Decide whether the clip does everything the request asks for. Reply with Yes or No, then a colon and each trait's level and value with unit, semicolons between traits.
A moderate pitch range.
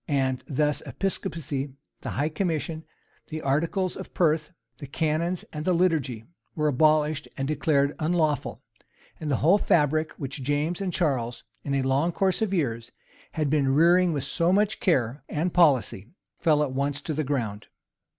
Yes: average, 3.3 semitones